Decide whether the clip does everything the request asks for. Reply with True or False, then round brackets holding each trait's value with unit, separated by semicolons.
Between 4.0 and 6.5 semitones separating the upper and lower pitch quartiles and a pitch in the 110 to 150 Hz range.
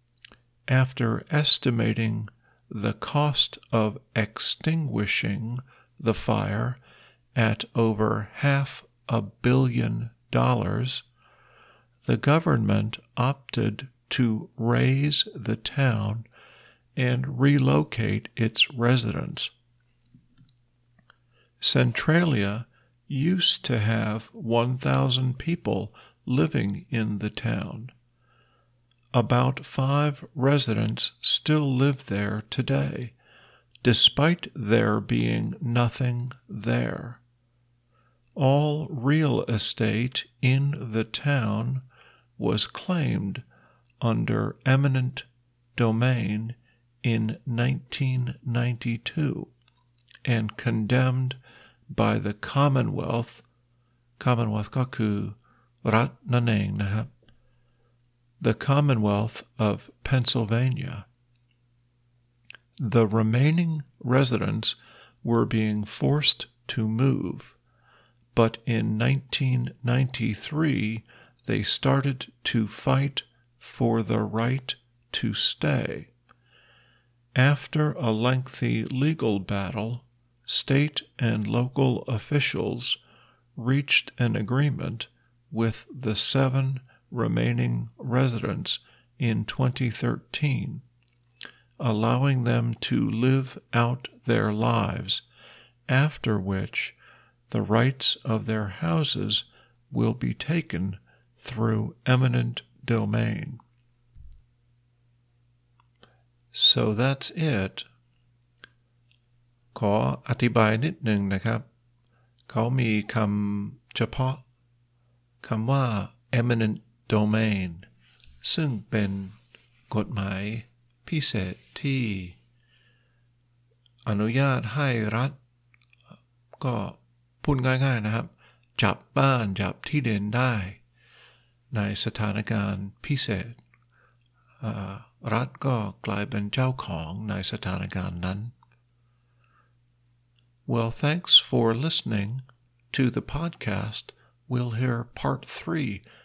False (2.6 semitones; 120 Hz)